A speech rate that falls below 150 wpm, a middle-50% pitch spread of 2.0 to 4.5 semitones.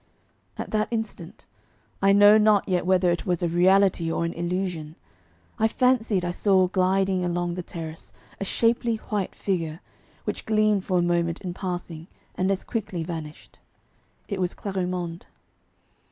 No: average, 155 wpm; narrow, 2.5 semitones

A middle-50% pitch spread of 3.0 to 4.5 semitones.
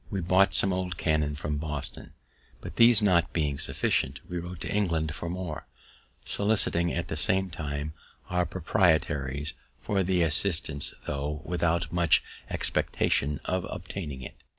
Yes: average, 3.6 semitones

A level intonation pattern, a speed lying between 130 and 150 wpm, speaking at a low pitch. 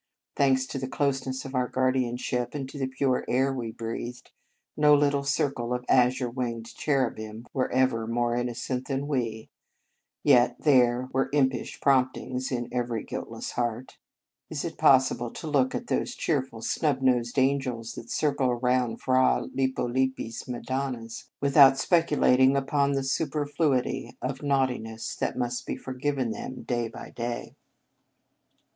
Yes: narrow, 2.2 semitones; average, 145 wpm; low, 130 Hz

